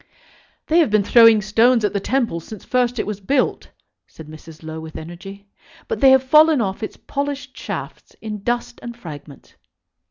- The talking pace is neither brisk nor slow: Yes, average, 180 wpm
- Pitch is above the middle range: Yes, high, 220 Hz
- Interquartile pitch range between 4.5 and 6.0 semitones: Yes, average, 5.2 semitones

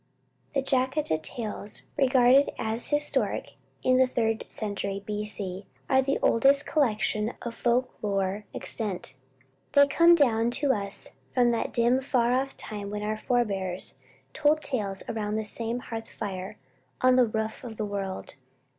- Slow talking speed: No, average, 150 wpm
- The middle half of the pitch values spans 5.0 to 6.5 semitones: No, average, 3.8 semitones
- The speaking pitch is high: Yes, high, 230 Hz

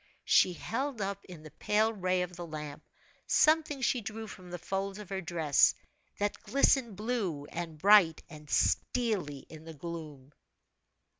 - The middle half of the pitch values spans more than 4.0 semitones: Yes, average, 5.1 semitones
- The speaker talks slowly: No, average, 155 wpm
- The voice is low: No, medium, 185 Hz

